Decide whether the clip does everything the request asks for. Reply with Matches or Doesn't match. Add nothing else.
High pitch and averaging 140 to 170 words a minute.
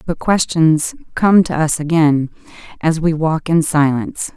Doesn't match